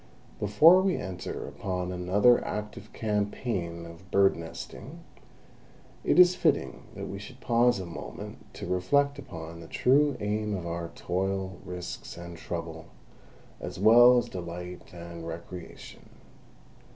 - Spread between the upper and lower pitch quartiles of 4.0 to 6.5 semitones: Yes, average, 5.2 semitones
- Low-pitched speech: Yes, very low, 95 Hz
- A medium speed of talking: No, slow, 130 wpm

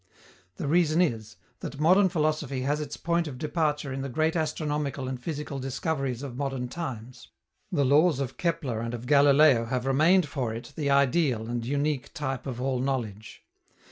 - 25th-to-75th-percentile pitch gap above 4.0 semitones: No, average, 3.4 semitones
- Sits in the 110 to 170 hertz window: Yes, medium, 140 Hz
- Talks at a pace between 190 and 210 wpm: No, average, 175 wpm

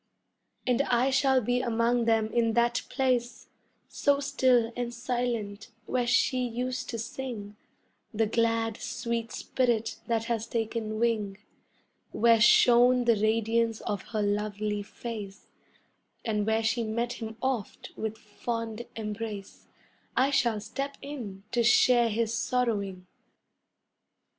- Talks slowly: Yes, slow, 125 wpm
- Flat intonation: Yes, narrow, 2.1 semitones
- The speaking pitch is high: Yes, high, 230 Hz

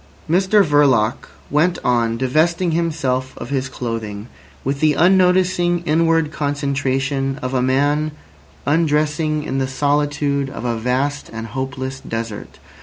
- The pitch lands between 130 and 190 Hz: Yes, medium, 140 Hz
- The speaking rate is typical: No, slow, 125 wpm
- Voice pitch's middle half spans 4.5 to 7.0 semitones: No, average, 3.2 semitones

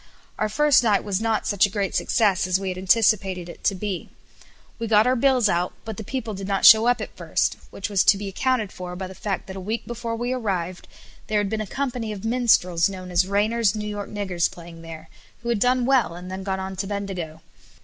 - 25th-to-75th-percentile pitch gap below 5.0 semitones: Yes, average, 3.4 semitones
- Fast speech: Yes, fast, 235 wpm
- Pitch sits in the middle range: No, high, 200 Hz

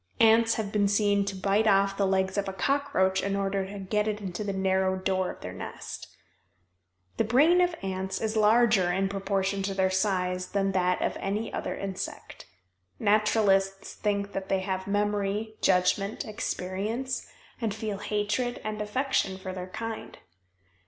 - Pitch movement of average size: No, narrow, 2.0 semitones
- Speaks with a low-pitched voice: No, high, 200 Hz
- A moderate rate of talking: Yes, average, 165 wpm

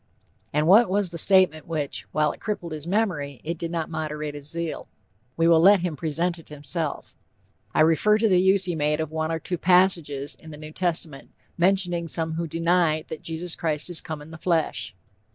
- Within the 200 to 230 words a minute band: Yes, fast, 205 wpm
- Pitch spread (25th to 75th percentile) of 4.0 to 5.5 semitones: No, narrow, 2.6 semitones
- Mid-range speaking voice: Yes, medium, 165 Hz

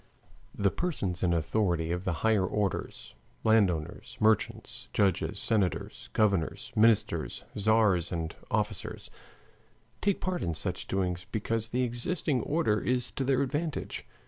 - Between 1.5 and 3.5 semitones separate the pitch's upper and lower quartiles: No, average, 5.0 semitones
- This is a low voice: Yes, low, 105 Hz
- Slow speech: Yes, slow, 125 wpm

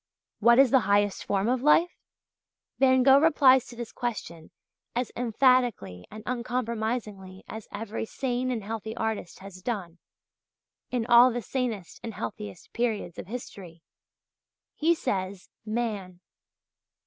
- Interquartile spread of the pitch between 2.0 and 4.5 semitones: Yes, average, 4.1 semitones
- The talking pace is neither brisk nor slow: No, slow, 130 wpm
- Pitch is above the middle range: Yes, high, 225 Hz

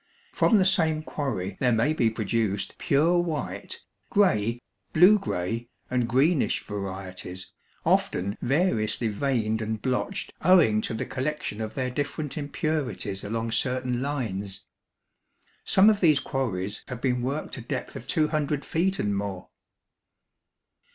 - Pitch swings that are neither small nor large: No, wide, 6.1 semitones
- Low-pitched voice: Yes, low, 125 Hz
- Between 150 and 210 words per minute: No, slow, 135 wpm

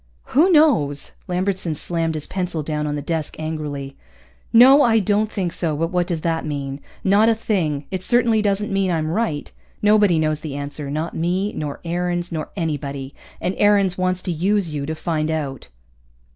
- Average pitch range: Yes, average, 4.6 semitones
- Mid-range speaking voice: Yes, medium, 170 Hz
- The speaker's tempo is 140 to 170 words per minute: No, average, 180 wpm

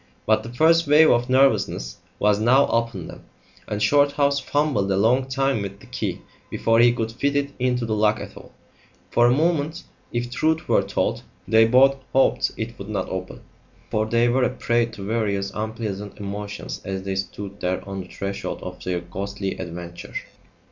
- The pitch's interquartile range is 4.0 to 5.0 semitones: Yes, average, 4.7 semitones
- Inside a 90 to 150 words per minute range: No, average, 180 wpm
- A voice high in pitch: No, low, 115 Hz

